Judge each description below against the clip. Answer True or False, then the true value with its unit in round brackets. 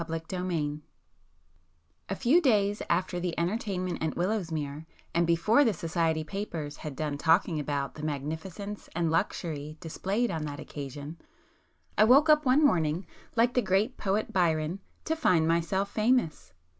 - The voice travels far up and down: False (4.8 semitones)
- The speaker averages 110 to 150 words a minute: True (145 wpm)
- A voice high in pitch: False (170 Hz)